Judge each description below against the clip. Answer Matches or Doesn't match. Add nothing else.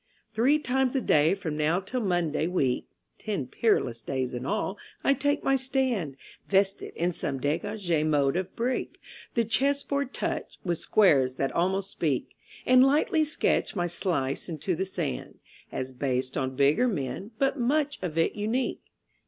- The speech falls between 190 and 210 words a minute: Doesn't match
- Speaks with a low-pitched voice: Doesn't match